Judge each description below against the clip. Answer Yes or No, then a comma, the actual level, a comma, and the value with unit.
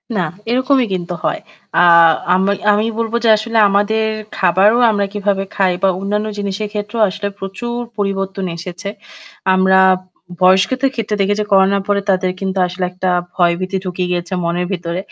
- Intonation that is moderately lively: No, narrow, 2.1 semitones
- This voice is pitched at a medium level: No, high, 195 Hz